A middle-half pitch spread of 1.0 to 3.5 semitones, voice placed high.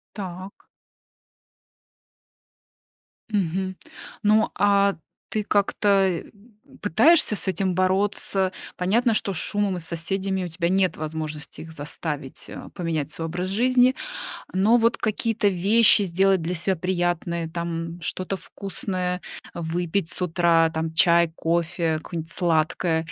No: average, 3.2 semitones; medium, 180 Hz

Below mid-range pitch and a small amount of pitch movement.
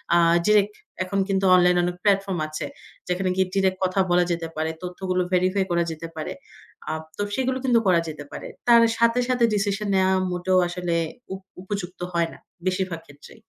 No: medium, 185 Hz; narrow, 2.0 semitones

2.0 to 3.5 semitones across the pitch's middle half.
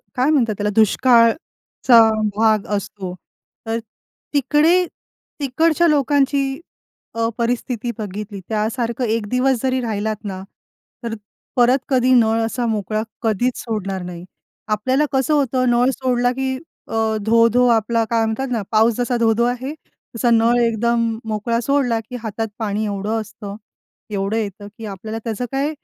Yes: average, 2.9 semitones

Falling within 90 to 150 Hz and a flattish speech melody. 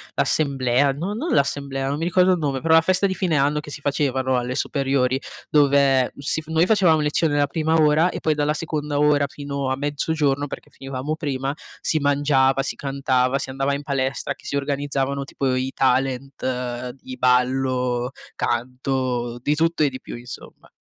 Yes: medium, 140 Hz; narrow, 2.2 semitones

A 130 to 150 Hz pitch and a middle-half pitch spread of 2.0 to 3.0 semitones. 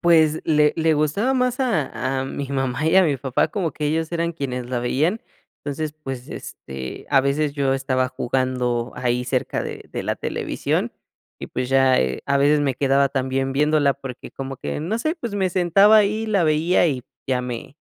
No: medium, 140 Hz; average, 3.7 semitones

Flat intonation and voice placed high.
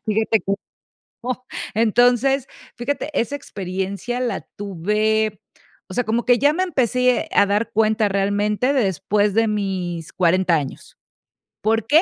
No: average, 3.8 semitones; high, 215 Hz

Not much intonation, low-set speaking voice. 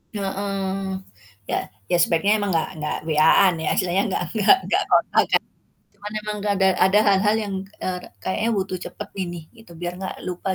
No: narrow, 2.1 semitones; high, 190 Hz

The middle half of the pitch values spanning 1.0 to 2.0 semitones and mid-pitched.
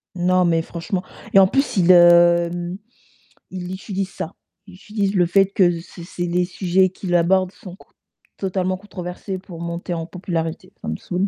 Yes: narrow, 1.6 semitones; medium, 180 Hz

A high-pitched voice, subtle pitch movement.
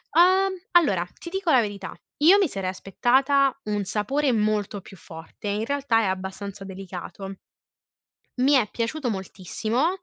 No: high, 215 Hz; wide, 6.4 semitones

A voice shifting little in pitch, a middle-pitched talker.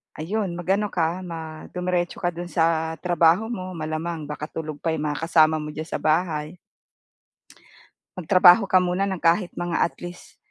Yes: narrow, 2.3 semitones; medium, 170 Hz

